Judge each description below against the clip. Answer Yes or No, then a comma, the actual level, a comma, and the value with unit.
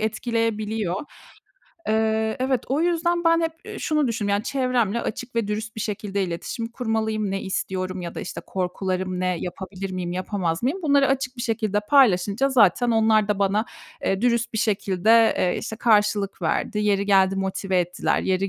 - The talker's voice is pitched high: Yes, high, 215 Hz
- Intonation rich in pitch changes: No, average, 3.6 semitones